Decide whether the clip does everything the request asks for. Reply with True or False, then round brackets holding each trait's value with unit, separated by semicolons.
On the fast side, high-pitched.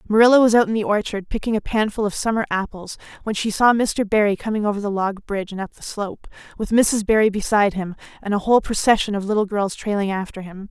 True (230 wpm; 210 Hz)